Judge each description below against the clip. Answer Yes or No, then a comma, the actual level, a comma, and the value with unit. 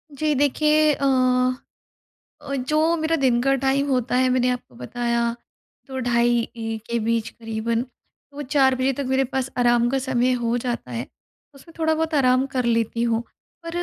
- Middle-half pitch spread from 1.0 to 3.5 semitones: Yes, average, 2.7 semitones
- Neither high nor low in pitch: No, very high, 255 Hz